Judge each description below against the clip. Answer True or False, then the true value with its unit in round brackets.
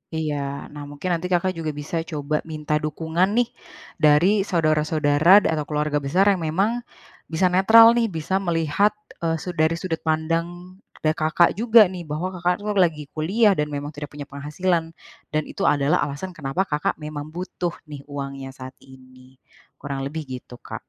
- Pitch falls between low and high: True (155 Hz)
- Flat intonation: False (3.4 semitones)